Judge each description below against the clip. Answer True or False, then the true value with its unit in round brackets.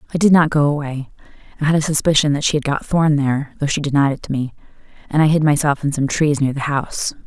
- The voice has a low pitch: False (145 Hz)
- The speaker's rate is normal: False (255 wpm)